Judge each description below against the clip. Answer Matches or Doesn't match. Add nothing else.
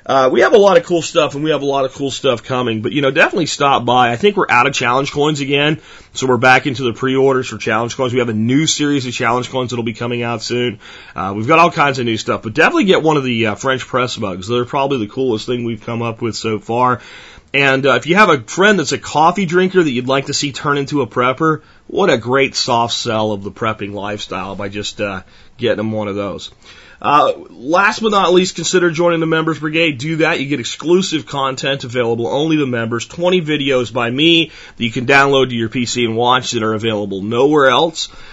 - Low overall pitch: Matches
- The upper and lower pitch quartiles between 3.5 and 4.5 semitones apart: Matches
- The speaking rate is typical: Doesn't match